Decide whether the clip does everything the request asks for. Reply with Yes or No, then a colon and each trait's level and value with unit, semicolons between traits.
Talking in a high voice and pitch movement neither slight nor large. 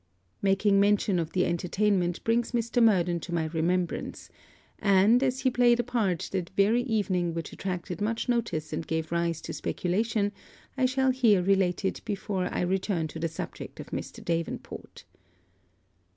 Yes: high, 195 Hz; average, 4.7 semitones